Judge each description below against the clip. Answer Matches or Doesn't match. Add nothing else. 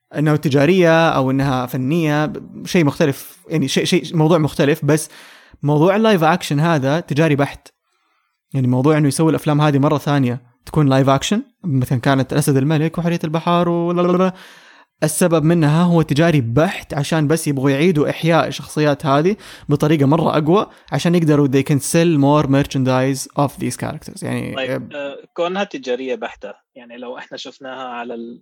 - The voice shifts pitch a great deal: Doesn't match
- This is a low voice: Doesn't match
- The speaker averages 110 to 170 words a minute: Matches